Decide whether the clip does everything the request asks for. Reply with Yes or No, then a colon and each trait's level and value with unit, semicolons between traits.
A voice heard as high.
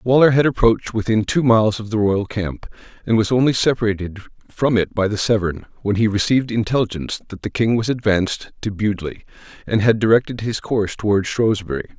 No: low, 110 Hz